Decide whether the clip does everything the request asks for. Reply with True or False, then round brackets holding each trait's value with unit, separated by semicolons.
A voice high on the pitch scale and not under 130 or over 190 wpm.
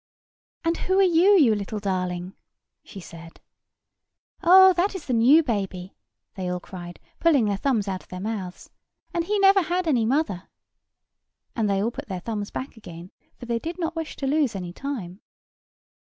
True (225 Hz; 180 wpm)